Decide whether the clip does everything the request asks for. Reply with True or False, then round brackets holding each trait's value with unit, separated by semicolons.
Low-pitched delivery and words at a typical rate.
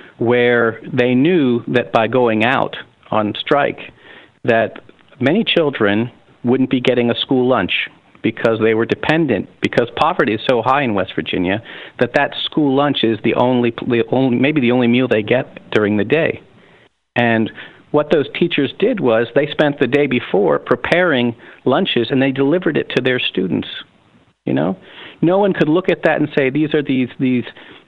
True (125 Hz; 175 wpm)